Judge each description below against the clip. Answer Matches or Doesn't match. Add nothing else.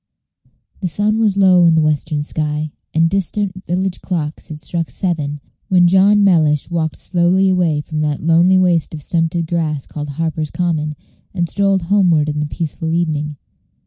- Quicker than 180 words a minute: Doesn't match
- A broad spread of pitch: Doesn't match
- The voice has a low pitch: Doesn't match